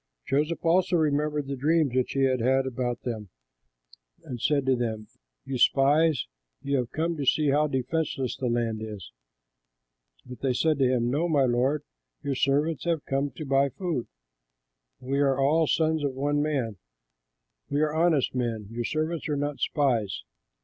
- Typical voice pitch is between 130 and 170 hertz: Yes, medium, 140 Hz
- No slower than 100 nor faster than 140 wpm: No, average, 170 wpm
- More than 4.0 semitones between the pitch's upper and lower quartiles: No, average, 3.3 semitones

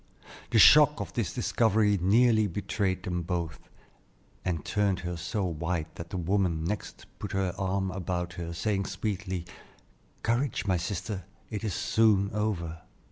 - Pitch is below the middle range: Yes, very low, 95 Hz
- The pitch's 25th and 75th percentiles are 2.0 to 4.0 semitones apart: Yes, average, 3.1 semitones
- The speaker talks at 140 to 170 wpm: Yes, average, 150 wpm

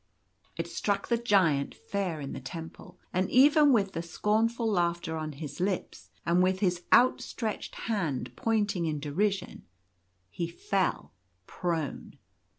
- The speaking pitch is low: No, medium, 185 Hz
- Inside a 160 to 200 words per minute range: No, slow, 135 wpm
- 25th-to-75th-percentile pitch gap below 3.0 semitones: No, average, 4.1 semitones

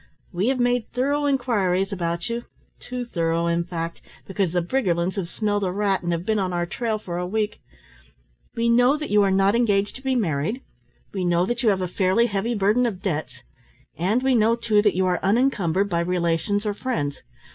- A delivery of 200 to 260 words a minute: Yes, fast, 205 wpm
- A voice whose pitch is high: Yes, high, 200 Hz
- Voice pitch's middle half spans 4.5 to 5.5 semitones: Yes, average, 4.8 semitones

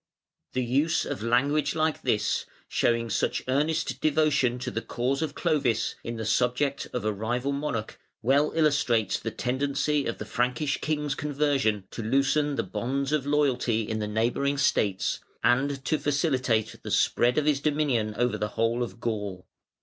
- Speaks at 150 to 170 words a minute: Yes, average, 165 wpm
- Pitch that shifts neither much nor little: Yes, average, 4.1 semitones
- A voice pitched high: No, low, 130 Hz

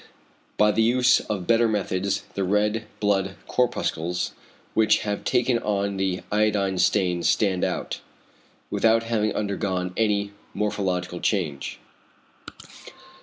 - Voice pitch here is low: Yes, low, 100 Hz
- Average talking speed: No, slow, 115 wpm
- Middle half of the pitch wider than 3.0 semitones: No, narrow, 2.6 semitones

